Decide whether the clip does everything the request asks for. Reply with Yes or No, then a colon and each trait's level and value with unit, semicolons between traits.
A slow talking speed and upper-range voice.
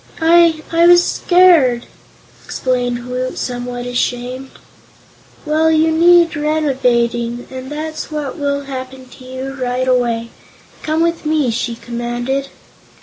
Yes: slow, 120 wpm; very high, 265 Hz